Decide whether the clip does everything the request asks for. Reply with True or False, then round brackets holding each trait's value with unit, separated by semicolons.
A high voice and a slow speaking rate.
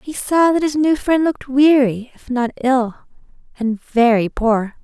False (260 Hz; 175 wpm)